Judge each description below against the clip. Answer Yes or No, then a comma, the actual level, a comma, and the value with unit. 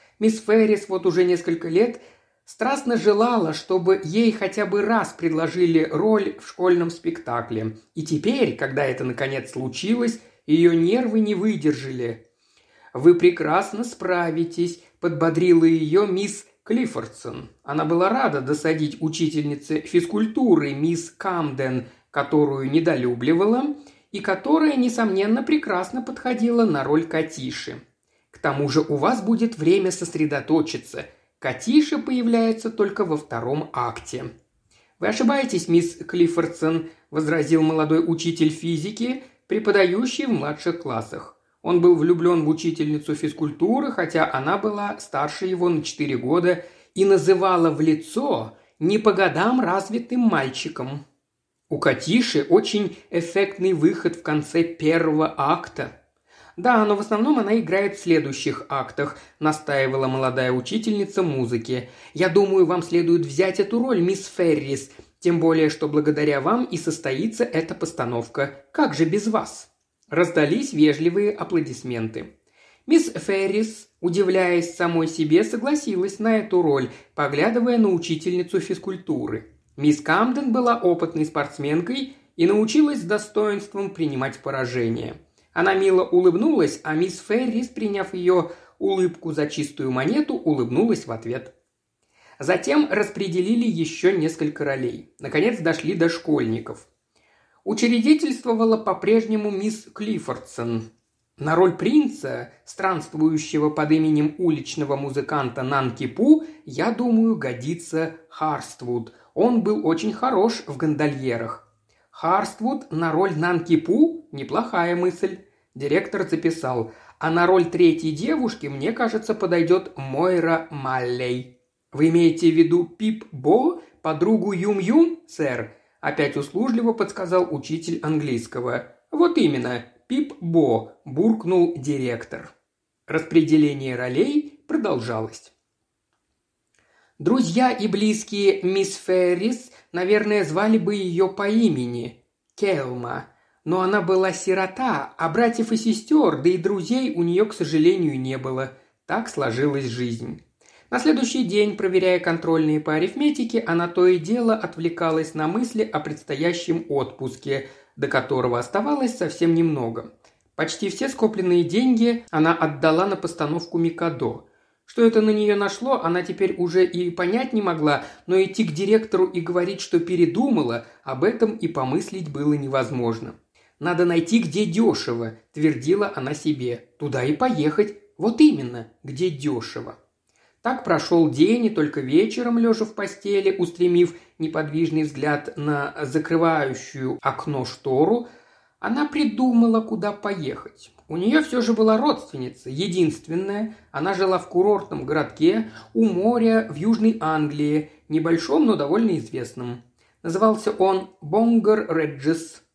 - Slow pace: No, average, 120 wpm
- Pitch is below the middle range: No, medium, 175 Hz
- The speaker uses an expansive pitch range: Yes, wide, 5.7 semitones